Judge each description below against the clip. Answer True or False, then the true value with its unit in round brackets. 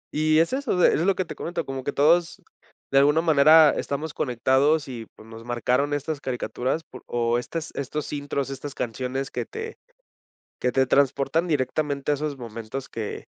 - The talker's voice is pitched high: False (140 Hz)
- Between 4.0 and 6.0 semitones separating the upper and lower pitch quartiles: False (3.5 semitones)